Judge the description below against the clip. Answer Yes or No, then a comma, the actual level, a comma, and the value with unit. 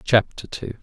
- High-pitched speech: No, low, 110 Hz